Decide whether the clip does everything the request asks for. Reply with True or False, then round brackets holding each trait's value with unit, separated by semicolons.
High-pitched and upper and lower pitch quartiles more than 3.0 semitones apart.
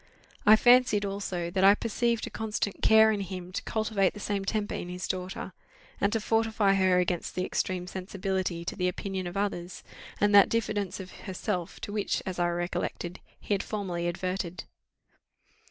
False (195 Hz; 2.4 semitones)